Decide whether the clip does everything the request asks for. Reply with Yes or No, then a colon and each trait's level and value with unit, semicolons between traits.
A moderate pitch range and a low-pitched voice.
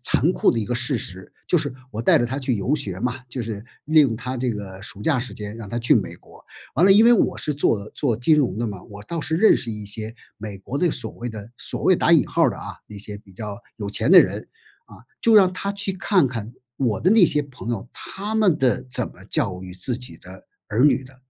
No: wide, 6.0 semitones; low, 120 Hz